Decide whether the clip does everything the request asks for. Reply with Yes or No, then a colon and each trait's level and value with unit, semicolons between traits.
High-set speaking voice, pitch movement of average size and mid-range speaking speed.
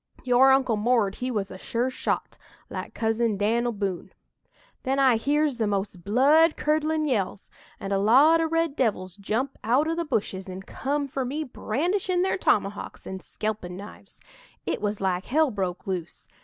No: high, 235 Hz; wide, 6.3 semitones; average, 170 wpm